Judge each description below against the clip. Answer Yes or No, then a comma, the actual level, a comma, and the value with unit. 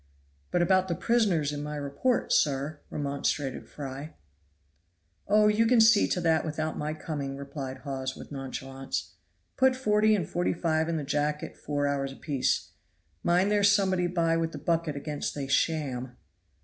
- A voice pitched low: No, medium, 155 Hz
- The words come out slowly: No, average, 155 wpm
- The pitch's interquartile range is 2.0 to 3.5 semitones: No, average, 4.2 semitones